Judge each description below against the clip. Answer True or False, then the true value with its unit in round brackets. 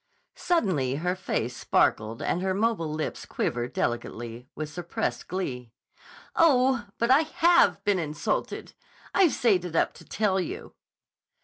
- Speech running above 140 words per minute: False (135 wpm)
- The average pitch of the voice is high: False (180 Hz)